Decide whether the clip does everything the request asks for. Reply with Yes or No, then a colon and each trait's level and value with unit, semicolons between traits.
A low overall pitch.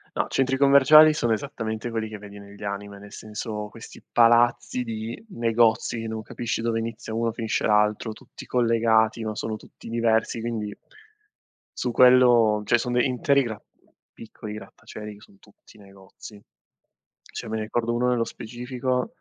Yes: low, 115 Hz